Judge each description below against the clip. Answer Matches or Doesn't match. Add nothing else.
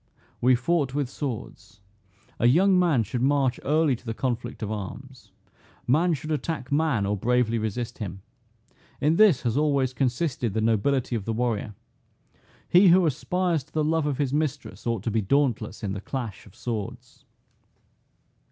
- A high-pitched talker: Doesn't match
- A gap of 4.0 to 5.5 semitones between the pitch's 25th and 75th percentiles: Matches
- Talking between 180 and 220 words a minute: Doesn't match